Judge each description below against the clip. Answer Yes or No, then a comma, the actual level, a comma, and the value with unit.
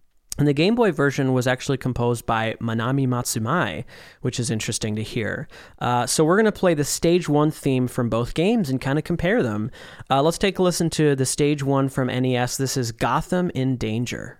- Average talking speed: No, fast, 210 wpm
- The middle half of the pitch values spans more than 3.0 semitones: Yes, average, 4.1 semitones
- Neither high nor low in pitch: No, low, 130 Hz